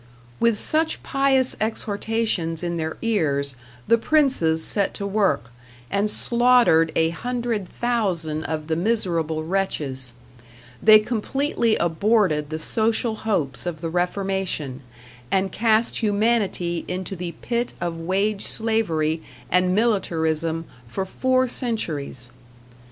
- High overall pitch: Yes, high, 195 Hz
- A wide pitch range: Yes, wide, 5.7 semitones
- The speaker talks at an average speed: No, slow, 115 wpm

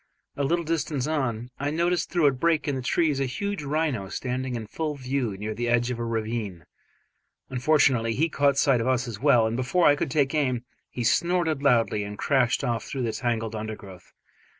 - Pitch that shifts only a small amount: No, average, 4.3 semitones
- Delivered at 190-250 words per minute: Yes, average, 200 wpm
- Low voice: Yes, low, 130 Hz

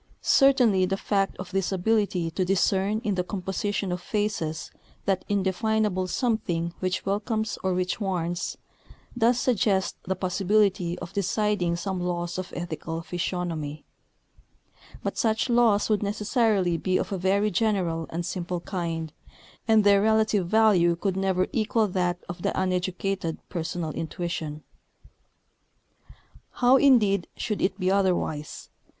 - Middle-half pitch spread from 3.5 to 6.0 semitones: No, average, 3.0 semitones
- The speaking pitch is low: No, high, 190 Hz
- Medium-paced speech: No, slow, 130 wpm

